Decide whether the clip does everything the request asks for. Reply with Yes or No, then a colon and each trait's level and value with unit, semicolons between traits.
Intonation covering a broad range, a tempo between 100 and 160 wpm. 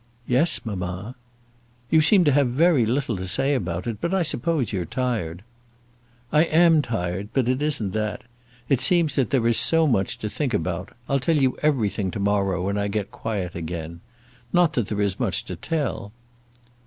No: wide, 6.9 semitones; average, 185 wpm